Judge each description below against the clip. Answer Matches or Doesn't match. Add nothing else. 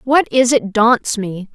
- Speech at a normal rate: Matches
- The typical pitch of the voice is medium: Doesn't match